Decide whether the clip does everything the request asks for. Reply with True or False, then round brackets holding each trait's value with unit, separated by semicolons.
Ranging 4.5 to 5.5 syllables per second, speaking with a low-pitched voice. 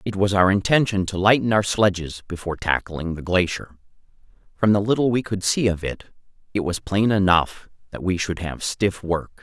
True (5.1 syllables/s; 95 Hz)